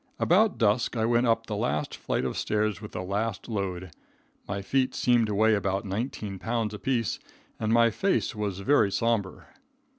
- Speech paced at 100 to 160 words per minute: No, average, 175 wpm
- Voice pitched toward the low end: Yes, low, 110 Hz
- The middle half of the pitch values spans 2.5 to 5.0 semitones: Yes, average, 2.8 semitones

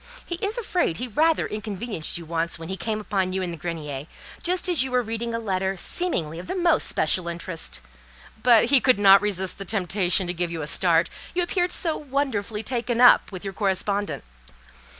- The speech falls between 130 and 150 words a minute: No, average, 200 wpm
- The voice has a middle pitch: No, high, 205 Hz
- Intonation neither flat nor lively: No, wide, 6.0 semitones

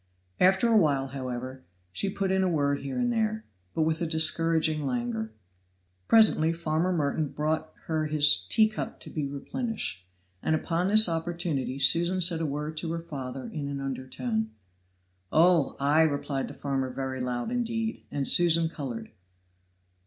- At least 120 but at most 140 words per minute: No, average, 160 wpm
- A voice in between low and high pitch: Yes, medium, 155 Hz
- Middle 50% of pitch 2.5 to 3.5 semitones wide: No, average, 4.2 semitones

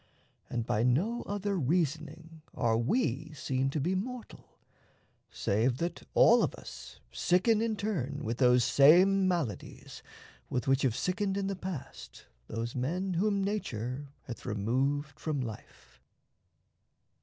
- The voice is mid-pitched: Yes, medium, 150 Hz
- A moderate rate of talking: No, slow, 130 wpm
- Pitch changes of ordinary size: No, wide, 7.3 semitones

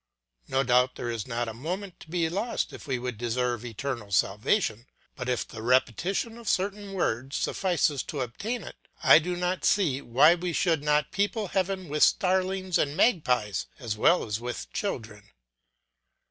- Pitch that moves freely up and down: Yes, wide, 7.4 semitones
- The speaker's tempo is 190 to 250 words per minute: No, average, 170 wpm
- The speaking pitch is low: No, medium, 145 Hz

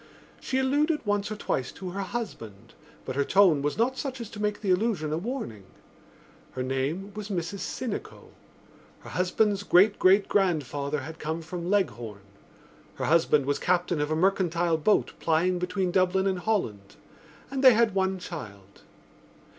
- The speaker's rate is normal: Yes, average, 160 wpm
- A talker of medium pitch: Yes, medium, 180 Hz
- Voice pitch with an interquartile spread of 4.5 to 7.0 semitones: Yes, average, 5.2 semitones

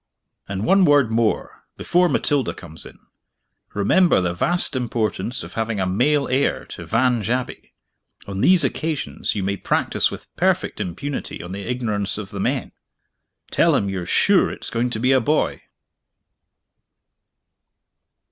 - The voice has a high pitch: No, low, 115 Hz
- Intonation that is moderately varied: No, wide, 5.8 semitones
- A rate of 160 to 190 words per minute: No, average, 145 wpm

